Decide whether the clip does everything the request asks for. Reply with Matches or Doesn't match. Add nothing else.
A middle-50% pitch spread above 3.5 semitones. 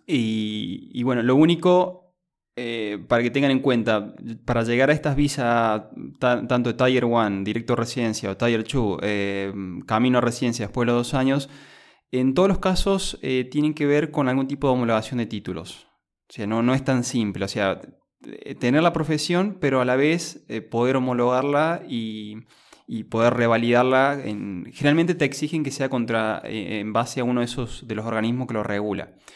Matches